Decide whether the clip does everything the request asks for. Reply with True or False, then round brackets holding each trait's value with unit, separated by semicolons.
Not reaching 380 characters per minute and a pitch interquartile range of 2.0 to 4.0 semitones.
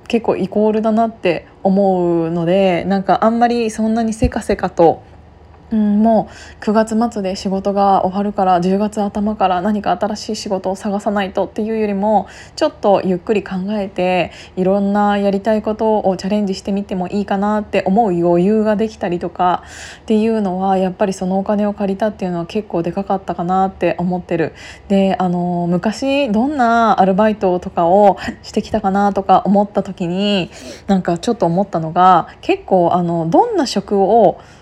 True (355 characters per minute; 2.7 semitones)